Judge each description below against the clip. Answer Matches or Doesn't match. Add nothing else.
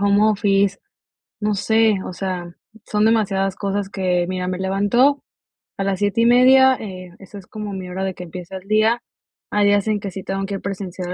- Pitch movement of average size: Doesn't match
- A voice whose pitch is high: Matches